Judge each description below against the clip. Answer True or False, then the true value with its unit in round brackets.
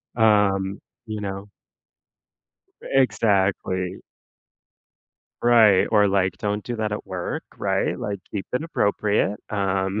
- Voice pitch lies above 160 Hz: False (100 Hz)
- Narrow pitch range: True (1.9 semitones)